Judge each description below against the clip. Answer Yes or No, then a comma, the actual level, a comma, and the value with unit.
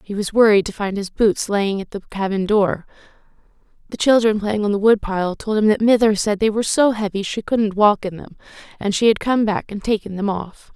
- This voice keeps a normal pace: No, fast, 230 wpm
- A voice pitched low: No, high, 205 Hz